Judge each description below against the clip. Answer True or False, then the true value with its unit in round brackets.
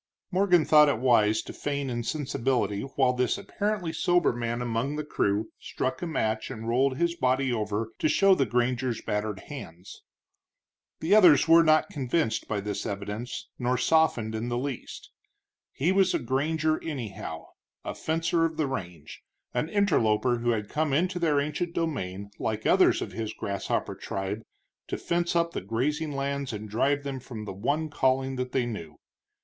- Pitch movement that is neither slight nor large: False (5.9 semitones)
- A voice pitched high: False (130 Hz)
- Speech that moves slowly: False (170 wpm)